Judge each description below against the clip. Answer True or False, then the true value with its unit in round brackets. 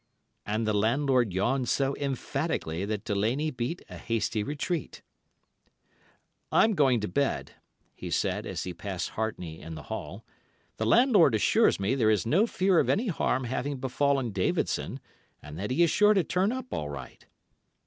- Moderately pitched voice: False (130 Hz)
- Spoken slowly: False (165 wpm)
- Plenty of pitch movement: True (6.6 semitones)